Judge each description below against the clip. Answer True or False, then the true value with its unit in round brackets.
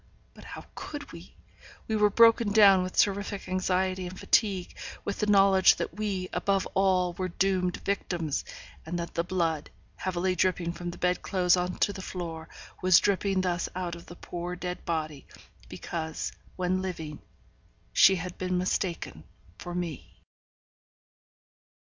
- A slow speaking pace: False (150 wpm)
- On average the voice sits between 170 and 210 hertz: True (185 Hz)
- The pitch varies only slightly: True (1.7 semitones)